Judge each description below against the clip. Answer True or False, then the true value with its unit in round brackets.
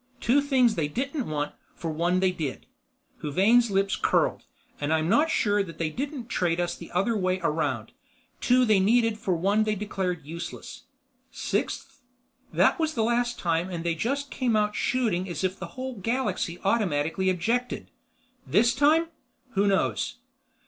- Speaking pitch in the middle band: False (200 Hz)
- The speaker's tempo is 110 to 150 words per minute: False (160 wpm)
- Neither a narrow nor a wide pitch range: False (5.7 semitones)